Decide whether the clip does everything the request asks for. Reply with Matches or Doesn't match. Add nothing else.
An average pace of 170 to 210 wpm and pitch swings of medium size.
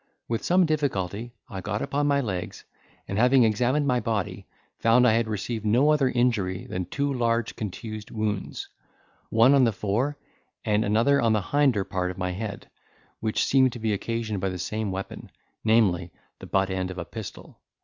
Matches